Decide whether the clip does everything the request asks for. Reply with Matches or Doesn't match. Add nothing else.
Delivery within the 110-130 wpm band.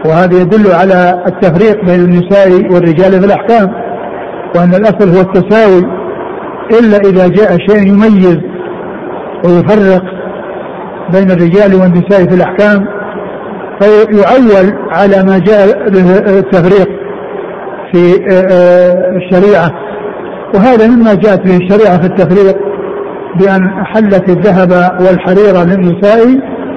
Doesn't match